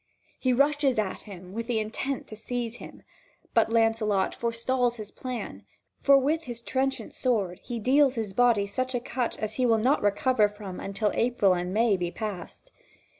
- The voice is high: Yes, high, 230 Hz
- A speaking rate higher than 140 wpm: Yes, average, 175 wpm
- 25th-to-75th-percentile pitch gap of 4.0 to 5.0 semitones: No, average, 3.6 semitones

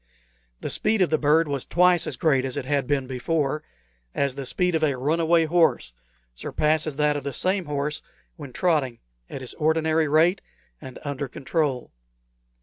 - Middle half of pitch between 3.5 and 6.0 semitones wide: No, average, 3.0 semitones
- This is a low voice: No, medium, 150 Hz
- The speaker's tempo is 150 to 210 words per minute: Yes, average, 170 wpm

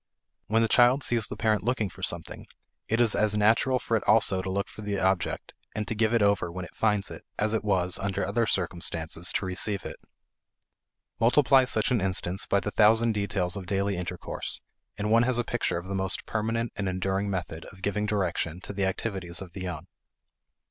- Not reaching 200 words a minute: No, fast, 205 wpm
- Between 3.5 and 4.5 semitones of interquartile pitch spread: No, average, 3.1 semitones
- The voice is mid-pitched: No, low, 100 Hz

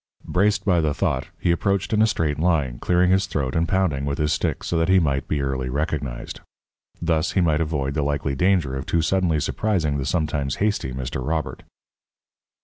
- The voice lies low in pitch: Yes, very low, 80 Hz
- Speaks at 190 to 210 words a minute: Yes, average, 195 wpm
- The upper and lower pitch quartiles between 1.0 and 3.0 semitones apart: No, average, 4.4 semitones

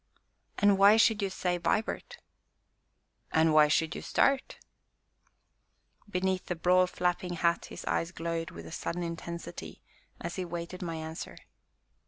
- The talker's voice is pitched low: No, medium, 175 Hz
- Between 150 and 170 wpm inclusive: No, average, 140 wpm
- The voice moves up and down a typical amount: No, narrow, 2.1 semitones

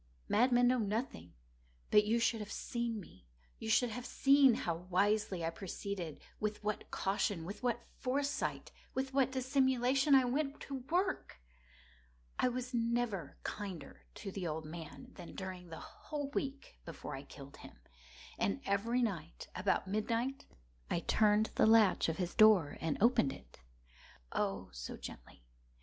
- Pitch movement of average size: No, wide, 6.5 semitones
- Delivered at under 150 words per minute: Yes, average, 140 wpm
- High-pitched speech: Yes, high, 210 Hz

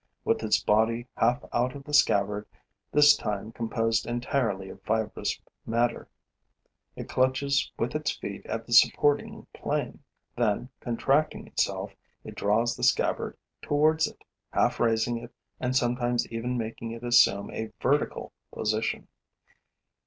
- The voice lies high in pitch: No, low, 120 Hz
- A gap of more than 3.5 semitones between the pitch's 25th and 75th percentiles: No, narrow, 2.5 semitones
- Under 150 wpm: Yes, slow, 135 wpm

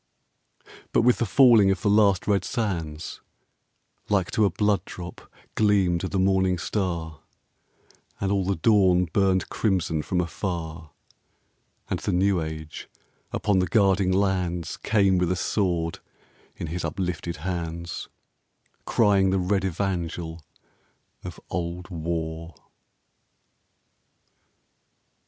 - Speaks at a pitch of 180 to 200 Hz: No, very low, 90 Hz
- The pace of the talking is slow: Yes, slow, 115 wpm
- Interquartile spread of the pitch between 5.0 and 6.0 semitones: No, average, 2.8 semitones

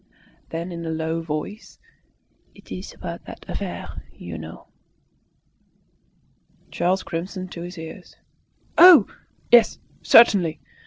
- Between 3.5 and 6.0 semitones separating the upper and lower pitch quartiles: No, average, 2.9 semitones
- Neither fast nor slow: No, slow, 105 wpm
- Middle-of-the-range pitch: Yes, medium, 170 Hz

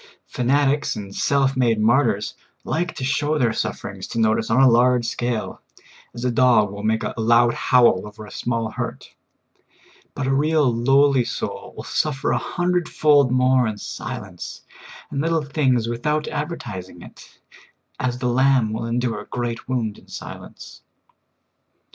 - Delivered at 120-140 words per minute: No, average, 155 wpm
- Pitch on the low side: Yes, low, 125 Hz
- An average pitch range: Yes, average, 3.3 semitones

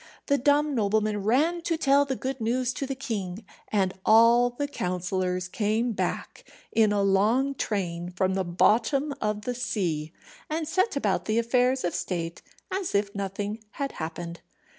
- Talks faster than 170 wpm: No, average, 160 wpm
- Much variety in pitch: Yes, wide, 5.8 semitones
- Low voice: No, high, 220 Hz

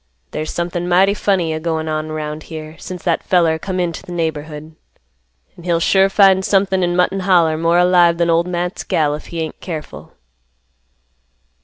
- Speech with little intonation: Yes, narrow, 2.3 semitones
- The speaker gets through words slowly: No, average, 175 wpm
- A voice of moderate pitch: Yes, medium, 170 Hz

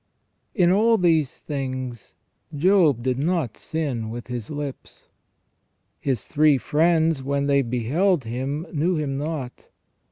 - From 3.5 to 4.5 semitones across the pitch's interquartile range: Yes, average, 4.0 semitones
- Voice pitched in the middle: Yes, medium, 145 Hz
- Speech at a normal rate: No, slow, 125 wpm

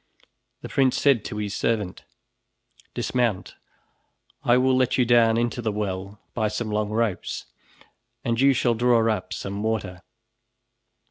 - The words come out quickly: No, average, 140 wpm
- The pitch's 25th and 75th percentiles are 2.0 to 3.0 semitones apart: Yes, narrow, 2.5 semitones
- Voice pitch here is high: No, low, 115 Hz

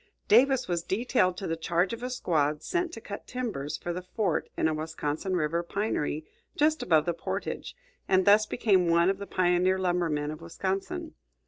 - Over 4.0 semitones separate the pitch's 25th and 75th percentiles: Yes, average, 4.6 semitones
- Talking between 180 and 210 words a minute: Yes, average, 185 wpm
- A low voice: No, medium, 185 Hz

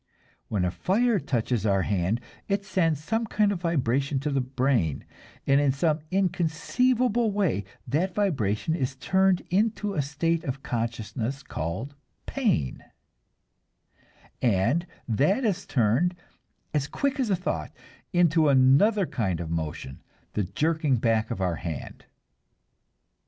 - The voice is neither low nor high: Yes, medium, 145 Hz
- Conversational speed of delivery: No, slow, 125 wpm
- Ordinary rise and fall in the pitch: No, wide, 8.7 semitones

